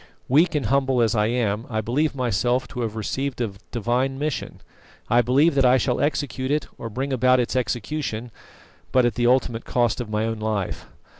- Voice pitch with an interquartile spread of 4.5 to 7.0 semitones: No, average, 2.9 semitones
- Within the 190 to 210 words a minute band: Yes, average, 195 wpm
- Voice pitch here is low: Yes, low, 125 Hz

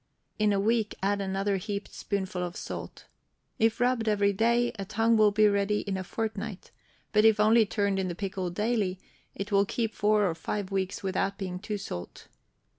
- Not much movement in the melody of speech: Yes, narrow, 2.0 semitones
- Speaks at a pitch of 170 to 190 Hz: No, high, 205 Hz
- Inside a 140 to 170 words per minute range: No, average, 190 wpm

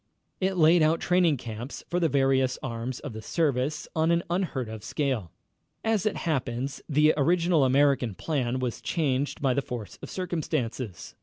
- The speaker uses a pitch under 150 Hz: Yes, medium, 140 Hz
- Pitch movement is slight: No, average, 4.8 semitones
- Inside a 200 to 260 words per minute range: No, average, 165 wpm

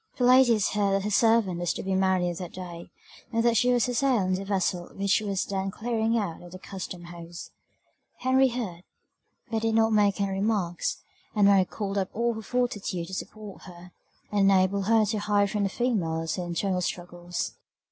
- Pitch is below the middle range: No, high, 200 Hz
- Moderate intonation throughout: Yes, average, 3.5 semitones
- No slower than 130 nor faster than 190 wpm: No, average, 200 wpm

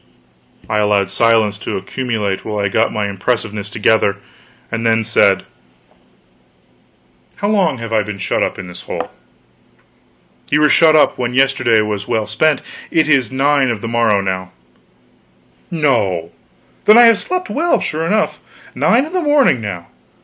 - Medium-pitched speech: No, low, 115 Hz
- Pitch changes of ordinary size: No, wide, 6.5 semitones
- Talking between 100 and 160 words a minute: Yes, average, 155 wpm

